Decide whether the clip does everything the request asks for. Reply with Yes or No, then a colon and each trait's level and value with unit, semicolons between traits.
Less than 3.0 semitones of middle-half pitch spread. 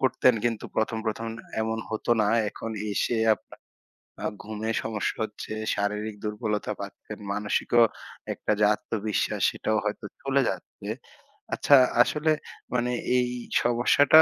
Yes: narrow, 2.4 semitones